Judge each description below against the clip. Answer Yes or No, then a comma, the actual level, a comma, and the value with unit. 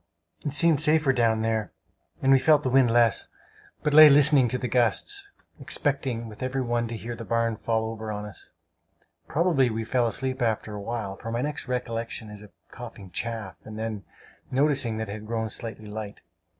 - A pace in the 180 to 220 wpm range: Yes, average, 190 wpm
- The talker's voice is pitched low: Yes, low, 115 Hz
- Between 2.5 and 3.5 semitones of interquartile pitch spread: Yes, average, 3.2 semitones